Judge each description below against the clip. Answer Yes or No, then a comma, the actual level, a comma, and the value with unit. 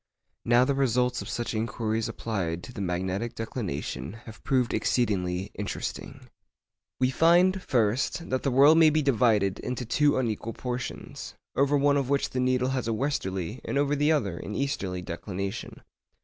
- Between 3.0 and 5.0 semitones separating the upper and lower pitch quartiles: No, wide, 5.6 semitones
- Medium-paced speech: Yes, average, 165 wpm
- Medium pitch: No, low, 120 Hz